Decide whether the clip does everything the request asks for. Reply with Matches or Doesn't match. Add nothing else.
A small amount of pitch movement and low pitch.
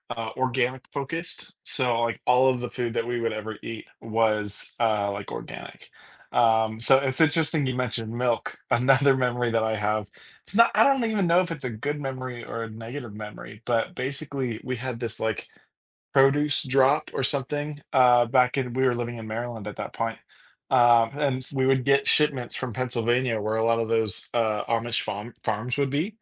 Doesn't match